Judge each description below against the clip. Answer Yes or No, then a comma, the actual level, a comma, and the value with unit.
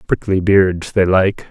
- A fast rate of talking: No, average, 160 wpm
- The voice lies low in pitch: Yes, very low, 95 Hz